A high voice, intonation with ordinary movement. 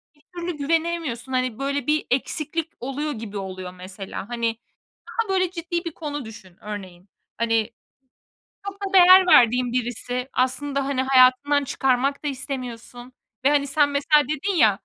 Yes: very high, 270 Hz; average, 4.6 semitones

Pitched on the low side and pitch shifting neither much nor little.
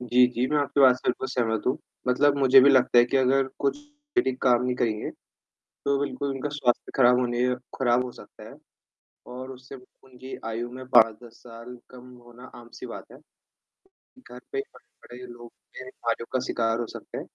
No: low, 125 Hz; narrow, 1.6 semitones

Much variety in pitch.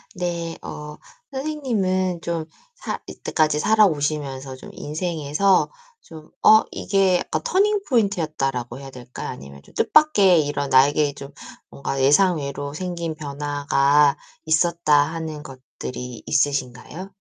No: average, 4.6 semitones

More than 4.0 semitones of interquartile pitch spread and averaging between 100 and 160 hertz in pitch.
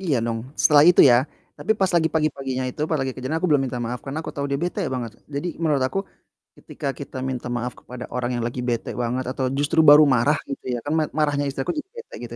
No: average, 3.4 semitones; medium, 140 Hz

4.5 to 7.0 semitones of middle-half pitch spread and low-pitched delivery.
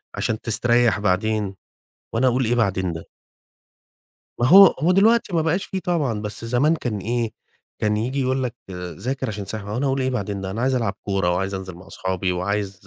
Yes: average, 4.9 semitones; low, 115 Hz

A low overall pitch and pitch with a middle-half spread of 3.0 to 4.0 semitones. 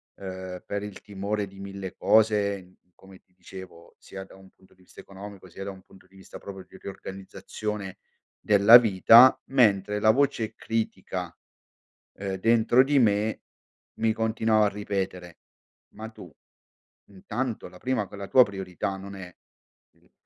No: low, 100 Hz; narrow, 2.4 semitones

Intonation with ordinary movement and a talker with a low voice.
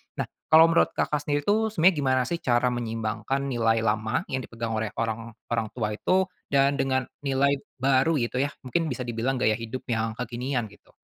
Yes: average, 3.6 semitones; low, 125 Hz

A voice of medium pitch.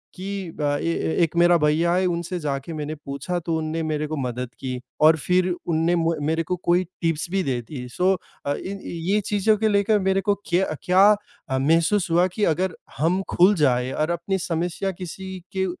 Yes: medium, 170 Hz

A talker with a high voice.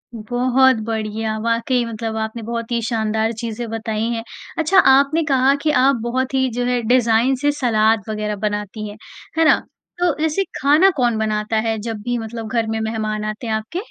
Yes: high, 230 Hz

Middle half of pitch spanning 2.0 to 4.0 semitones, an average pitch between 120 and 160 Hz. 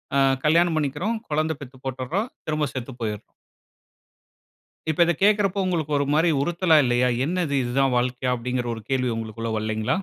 No: wide, 5.4 semitones; medium, 140 Hz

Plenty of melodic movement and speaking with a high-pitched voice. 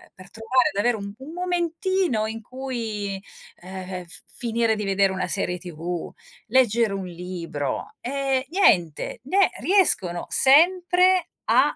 Yes: wide, 7.2 semitones; high, 225 Hz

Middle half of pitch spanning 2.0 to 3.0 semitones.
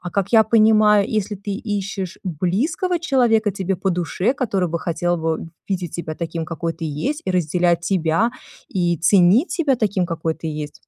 No: average, 4.2 semitones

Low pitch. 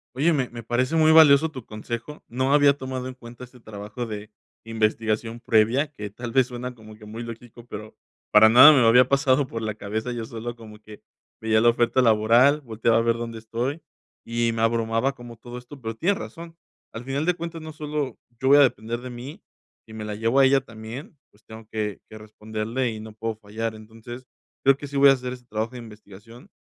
Yes: low, 120 Hz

